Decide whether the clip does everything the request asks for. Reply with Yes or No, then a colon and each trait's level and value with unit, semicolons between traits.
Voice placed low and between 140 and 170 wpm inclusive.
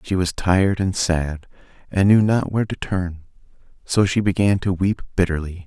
No: very low, 90 Hz; average, 180 wpm